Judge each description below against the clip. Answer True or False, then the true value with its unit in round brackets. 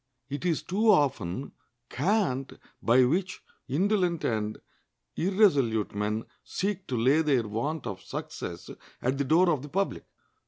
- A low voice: False (145 Hz)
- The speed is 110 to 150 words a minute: True (135 wpm)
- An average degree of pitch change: False (7.6 semitones)